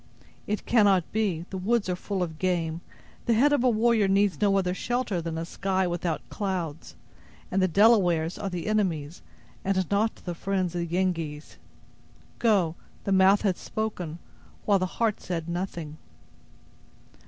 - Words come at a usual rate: Yes, average, 160 wpm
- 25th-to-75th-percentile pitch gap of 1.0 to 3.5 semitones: Yes, average, 3.2 semitones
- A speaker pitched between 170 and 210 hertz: Yes, medium, 185 Hz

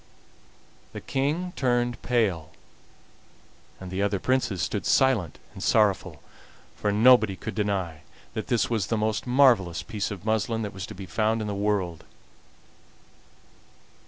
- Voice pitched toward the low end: Yes, low, 105 Hz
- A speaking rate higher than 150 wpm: No, average, 140 wpm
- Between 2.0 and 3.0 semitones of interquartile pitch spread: No, average, 3.9 semitones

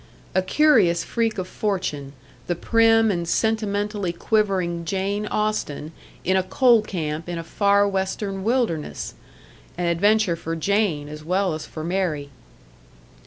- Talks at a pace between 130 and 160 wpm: Yes, slow, 135 wpm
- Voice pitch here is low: No, high, 190 Hz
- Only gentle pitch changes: No, average, 3.9 semitones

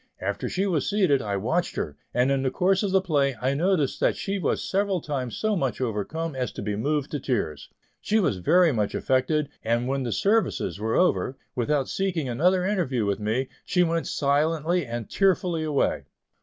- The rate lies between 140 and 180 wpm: No, average, 195 wpm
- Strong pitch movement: Yes, wide, 6.5 semitones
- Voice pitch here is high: No, medium, 145 Hz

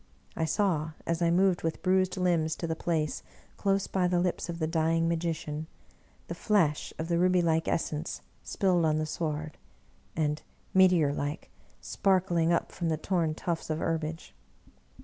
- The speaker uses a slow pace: No, average, 160 wpm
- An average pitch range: No, narrow, 2.3 semitones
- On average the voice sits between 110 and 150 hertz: No, medium, 165 Hz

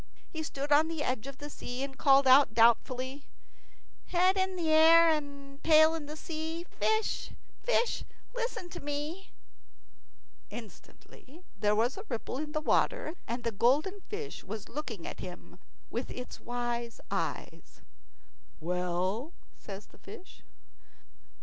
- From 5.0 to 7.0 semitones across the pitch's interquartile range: Yes, wide, 5.5 semitones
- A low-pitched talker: No, very high, 285 Hz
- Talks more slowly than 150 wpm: Yes, slow, 135 wpm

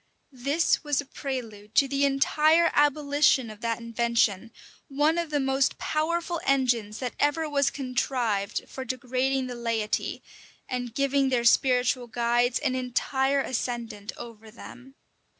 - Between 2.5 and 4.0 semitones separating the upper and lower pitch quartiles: Yes, average, 3.0 semitones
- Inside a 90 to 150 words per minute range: Yes, average, 140 wpm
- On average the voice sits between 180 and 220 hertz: No, very high, 255 Hz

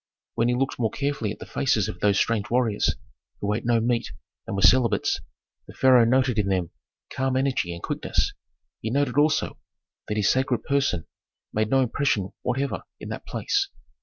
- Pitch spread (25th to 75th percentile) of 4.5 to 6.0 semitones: No, average, 4.0 semitones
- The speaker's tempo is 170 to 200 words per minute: Yes, average, 180 wpm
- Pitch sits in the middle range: No, low, 120 Hz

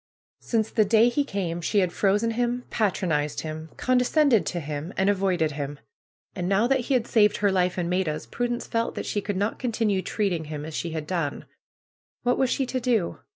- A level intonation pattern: No, wide, 5.6 semitones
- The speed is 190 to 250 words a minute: Yes, average, 200 wpm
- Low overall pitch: No, high, 200 Hz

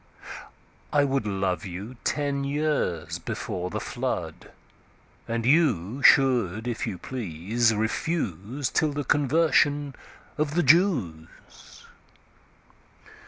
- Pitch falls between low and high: No, low, 125 Hz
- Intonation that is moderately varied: No, wide, 6.8 semitones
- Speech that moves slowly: Yes, slow, 85 wpm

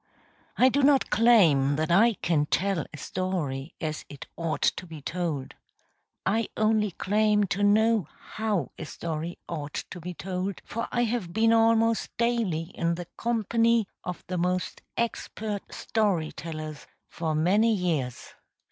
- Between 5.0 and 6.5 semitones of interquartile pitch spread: Yes, wide, 5.4 semitones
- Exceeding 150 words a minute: No, average, 145 wpm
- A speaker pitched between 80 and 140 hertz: No, medium, 185 Hz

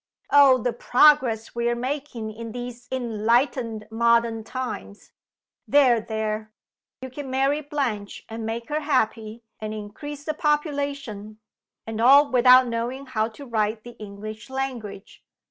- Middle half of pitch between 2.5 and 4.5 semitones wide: Yes, average, 3.6 semitones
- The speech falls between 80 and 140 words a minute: Yes, slow, 135 wpm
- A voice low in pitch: No, high, 235 Hz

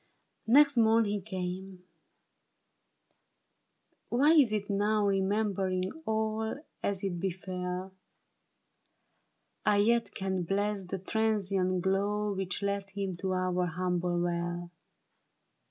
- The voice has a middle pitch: No, high, 195 Hz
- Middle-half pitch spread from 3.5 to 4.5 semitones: No, narrow, 2.4 semitones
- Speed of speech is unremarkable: No, slow, 105 wpm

